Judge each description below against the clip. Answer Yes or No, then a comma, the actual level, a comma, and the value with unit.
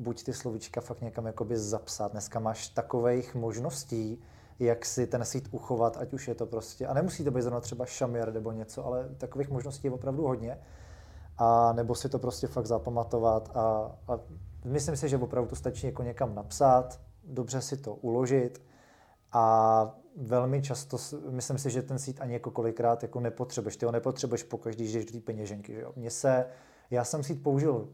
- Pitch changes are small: Yes, narrow, 2.2 semitones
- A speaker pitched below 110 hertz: No, low, 120 Hz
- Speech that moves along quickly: Yes, fast, 190 wpm